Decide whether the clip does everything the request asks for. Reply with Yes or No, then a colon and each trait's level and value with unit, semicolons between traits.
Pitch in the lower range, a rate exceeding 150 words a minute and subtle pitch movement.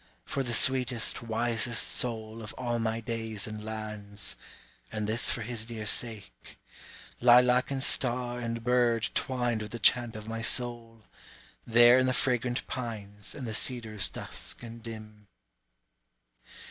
No: low, 115 Hz; average, 145 wpm; narrow, 2.0 semitones